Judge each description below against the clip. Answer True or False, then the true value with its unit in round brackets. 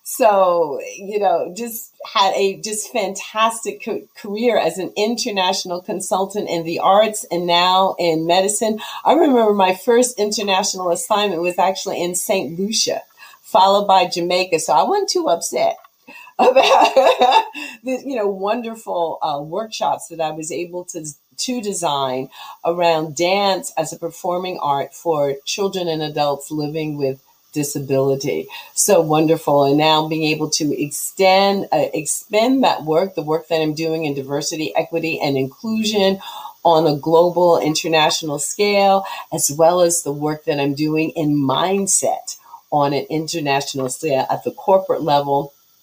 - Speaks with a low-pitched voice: False (175 Hz)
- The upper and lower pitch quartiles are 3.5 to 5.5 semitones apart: True (4.7 semitones)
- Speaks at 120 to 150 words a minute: True (145 wpm)